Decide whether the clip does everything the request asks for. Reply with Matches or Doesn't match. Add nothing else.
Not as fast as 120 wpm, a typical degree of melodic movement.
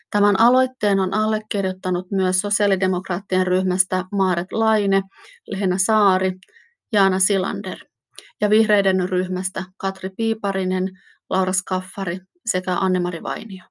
Doesn't match